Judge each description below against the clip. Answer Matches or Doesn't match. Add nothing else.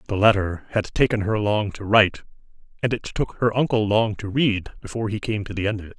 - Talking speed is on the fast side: Matches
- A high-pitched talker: Doesn't match